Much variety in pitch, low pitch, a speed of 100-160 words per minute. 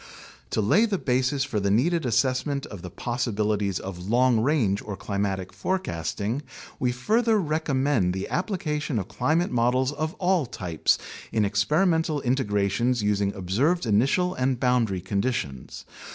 Yes: wide, 6.6 semitones; low, 125 Hz; average, 140 wpm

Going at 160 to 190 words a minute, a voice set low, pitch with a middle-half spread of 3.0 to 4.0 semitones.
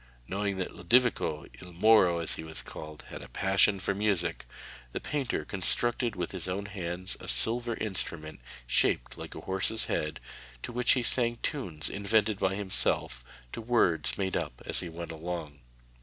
No: average, 170 wpm; very low, 95 Hz; average, 4.6 semitones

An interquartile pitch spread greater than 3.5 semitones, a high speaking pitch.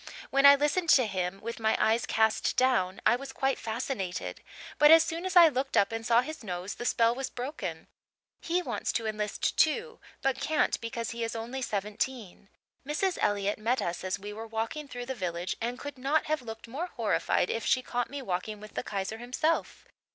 Yes: average, 4.5 semitones; high, 235 Hz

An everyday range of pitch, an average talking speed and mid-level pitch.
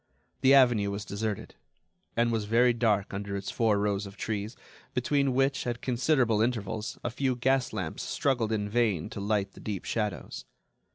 No: average, 3.2 semitones; average, 170 wpm; low, 110 Hz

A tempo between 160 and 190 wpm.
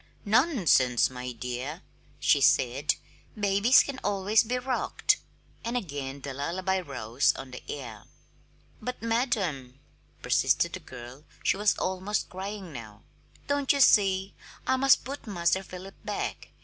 No: slow, 135 wpm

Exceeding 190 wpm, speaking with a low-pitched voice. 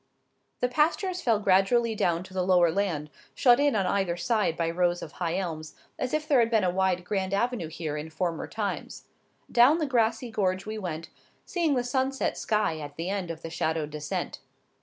No: average, 200 wpm; high, 190 Hz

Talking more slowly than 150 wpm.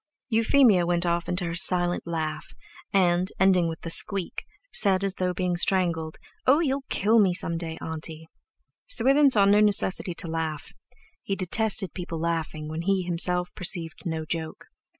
No: average, 160 wpm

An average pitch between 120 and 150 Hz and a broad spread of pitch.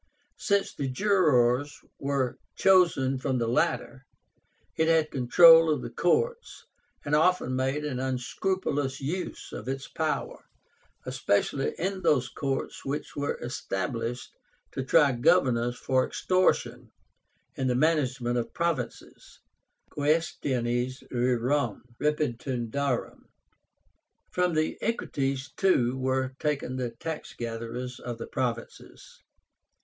No: low, 135 Hz; average, 4.0 semitones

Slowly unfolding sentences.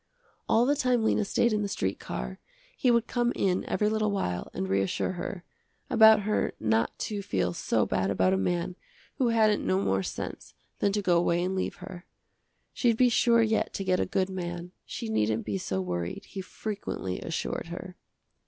No: average, 190 wpm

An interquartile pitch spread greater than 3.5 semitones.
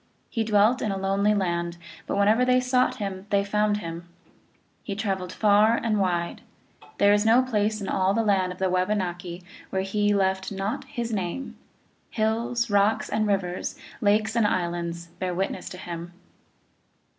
No: average, 2.9 semitones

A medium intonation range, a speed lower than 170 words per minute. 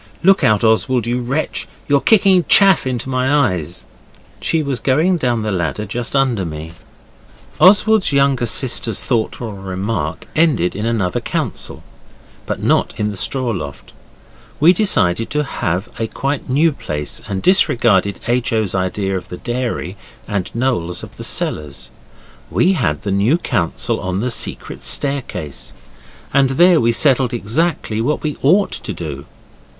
No: wide, 6.5 semitones; average, 150 wpm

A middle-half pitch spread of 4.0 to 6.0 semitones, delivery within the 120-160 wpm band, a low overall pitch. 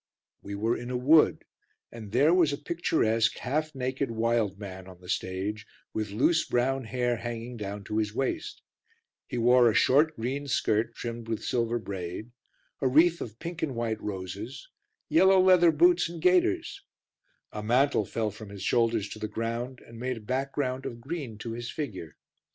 No: average, 4.7 semitones; average, 175 wpm; low, 120 Hz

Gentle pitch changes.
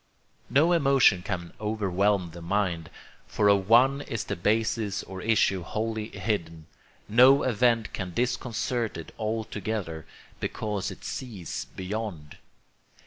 No: average, 3.7 semitones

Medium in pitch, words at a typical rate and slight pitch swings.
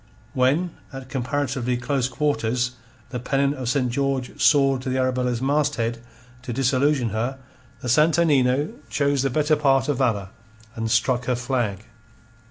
No: low, 130 Hz; average, 150 wpm; narrow, 2.3 semitones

